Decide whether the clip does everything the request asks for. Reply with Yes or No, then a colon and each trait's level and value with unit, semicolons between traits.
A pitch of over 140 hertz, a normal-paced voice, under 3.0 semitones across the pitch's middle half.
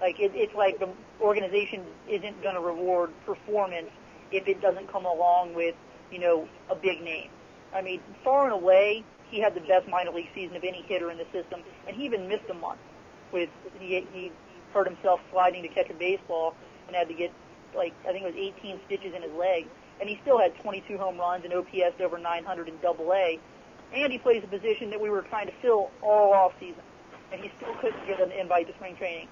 No: medium, 185 Hz; fast, 220 wpm; narrow, 2.4 semitones